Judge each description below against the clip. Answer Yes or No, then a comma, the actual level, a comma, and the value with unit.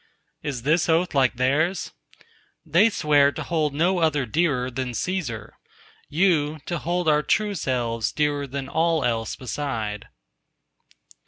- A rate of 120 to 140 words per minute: Yes, slow, 135 wpm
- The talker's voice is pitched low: No, medium, 150 Hz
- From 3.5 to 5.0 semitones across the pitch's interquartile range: Yes, average, 4.6 semitones